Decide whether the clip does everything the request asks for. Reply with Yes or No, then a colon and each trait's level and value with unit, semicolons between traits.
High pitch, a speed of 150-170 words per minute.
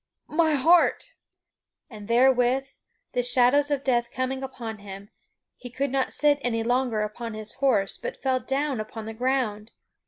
Yes: high, 245 Hz; average, 155 wpm